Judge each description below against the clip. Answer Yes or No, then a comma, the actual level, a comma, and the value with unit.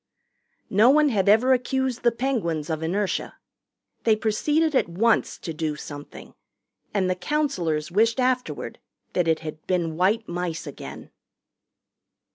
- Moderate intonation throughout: No, wide, 7.1 semitones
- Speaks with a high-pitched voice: Yes, high, 200 Hz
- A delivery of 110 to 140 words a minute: Yes, slow, 135 wpm